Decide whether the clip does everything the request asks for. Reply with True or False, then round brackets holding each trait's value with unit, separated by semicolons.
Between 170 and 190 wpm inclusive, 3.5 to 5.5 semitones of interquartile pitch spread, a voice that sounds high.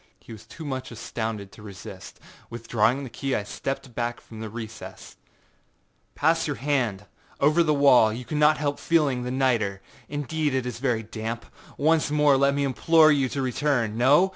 False (185 wpm; 4.2 semitones; 130 Hz)